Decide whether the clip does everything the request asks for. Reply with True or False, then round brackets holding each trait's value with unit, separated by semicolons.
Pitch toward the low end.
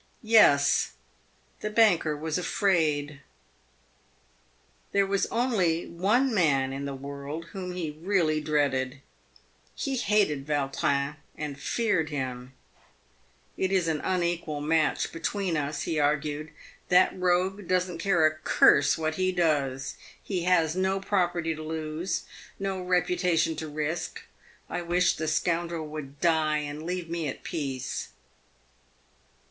False (160 Hz)